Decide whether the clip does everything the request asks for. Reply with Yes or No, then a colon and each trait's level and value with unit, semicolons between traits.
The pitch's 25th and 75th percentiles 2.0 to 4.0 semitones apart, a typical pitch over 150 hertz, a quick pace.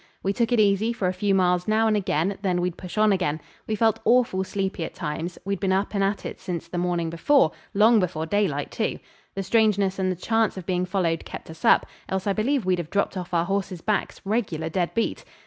Yes: average, 2.9 semitones; high, 190 Hz; fast, 235 wpm